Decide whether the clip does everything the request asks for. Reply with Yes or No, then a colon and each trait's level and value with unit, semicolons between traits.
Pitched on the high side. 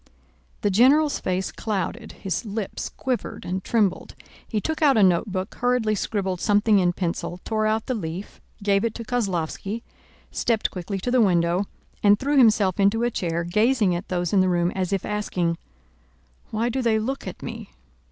Yes: high, 205 Hz